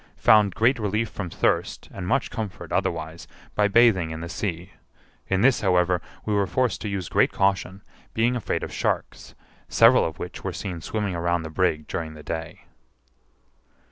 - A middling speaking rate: Yes, average, 170 wpm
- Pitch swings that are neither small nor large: Yes, average, 4.0 semitones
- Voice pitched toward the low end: Yes, very low, 95 Hz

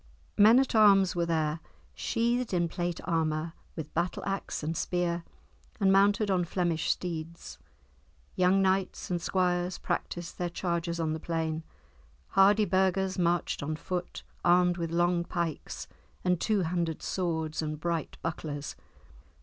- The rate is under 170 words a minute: Yes, average, 140 wpm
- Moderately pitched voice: Yes, medium, 175 Hz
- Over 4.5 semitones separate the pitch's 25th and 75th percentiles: No, narrow, 2.4 semitones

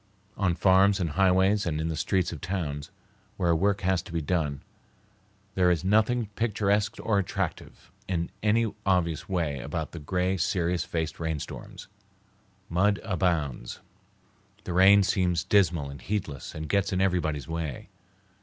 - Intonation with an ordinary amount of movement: Yes, average, 3.4 semitones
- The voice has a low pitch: Yes, very low, 90 Hz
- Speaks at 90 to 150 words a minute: Yes, average, 145 wpm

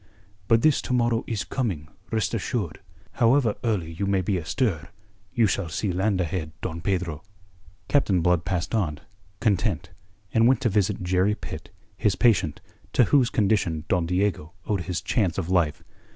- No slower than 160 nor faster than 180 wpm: Yes, average, 165 wpm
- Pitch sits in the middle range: No, very low, 95 Hz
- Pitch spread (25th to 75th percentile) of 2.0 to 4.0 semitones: No, average, 4.5 semitones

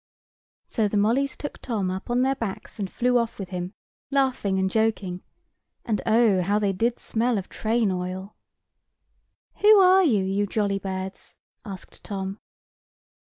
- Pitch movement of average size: Yes, average, 3.9 semitones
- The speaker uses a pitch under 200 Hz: No, high, 210 Hz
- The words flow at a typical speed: Yes, average, 150 wpm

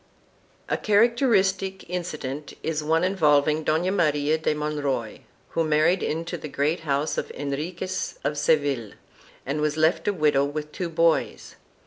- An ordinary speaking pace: Yes, average, 150 wpm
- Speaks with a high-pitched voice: No, medium, 155 Hz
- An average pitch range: Yes, average, 3.1 semitones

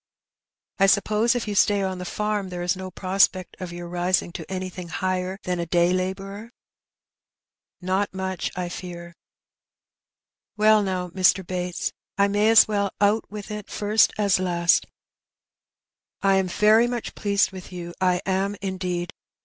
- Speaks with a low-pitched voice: No, high, 190 Hz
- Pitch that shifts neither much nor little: No, narrow, 2.2 semitones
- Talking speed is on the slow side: No, average, 160 wpm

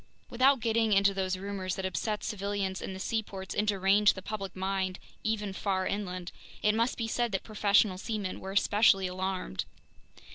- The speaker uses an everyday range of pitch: No, narrow, 2.1 semitones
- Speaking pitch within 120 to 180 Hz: No, high, 195 Hz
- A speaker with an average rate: Yes, average, 170 wpm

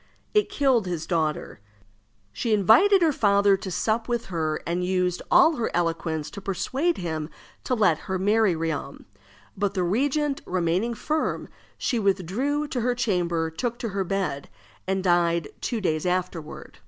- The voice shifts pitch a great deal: Yes, wide, 5.7 semitones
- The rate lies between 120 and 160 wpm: Yes, average, 155 wpm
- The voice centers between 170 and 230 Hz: Yes, high, 190 Hz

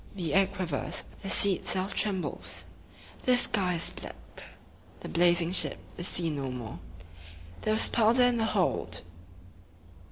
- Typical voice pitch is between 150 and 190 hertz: Yes, medium, 185 Hz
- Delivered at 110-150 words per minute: Yes, average, 140 wpm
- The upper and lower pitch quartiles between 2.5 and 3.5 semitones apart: No, average, 4.0 semitones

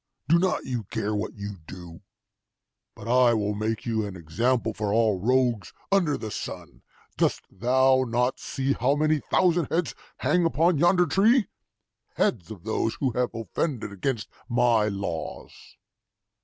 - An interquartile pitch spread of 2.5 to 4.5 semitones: No, average, 5.2 semitones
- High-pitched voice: No, low, 120 Hz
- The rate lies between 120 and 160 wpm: Yes, average, 150 wpm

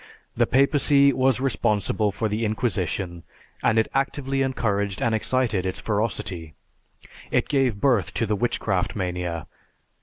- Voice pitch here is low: Yes, low, 110 Hz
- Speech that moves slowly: Yes, slow, 130 wpm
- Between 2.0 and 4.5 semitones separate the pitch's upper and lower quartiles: No, average, 5.1 semitones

